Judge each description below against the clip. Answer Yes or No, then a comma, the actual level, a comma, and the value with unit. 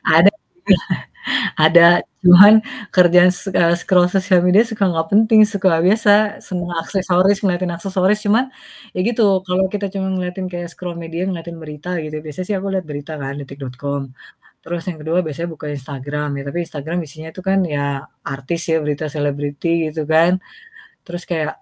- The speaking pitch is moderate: Yes, medium, 175 Hz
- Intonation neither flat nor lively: Yes, average, 3.3 semitones